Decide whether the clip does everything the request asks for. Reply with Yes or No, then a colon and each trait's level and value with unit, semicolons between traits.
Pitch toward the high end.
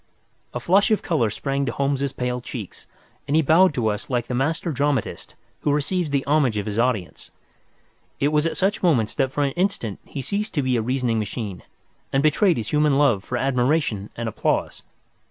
No: low, 135 Hz